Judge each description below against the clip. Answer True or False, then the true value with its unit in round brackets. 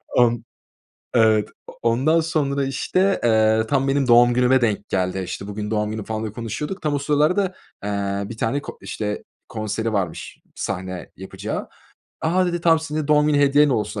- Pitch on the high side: False (120 Hz)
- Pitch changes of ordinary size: False (5.7 semitones)